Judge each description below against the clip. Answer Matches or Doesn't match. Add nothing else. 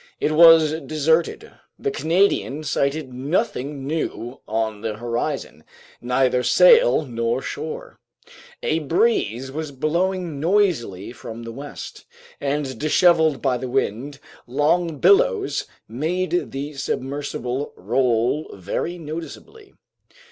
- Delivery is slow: Matches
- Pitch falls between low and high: Matches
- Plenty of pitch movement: Doesn't match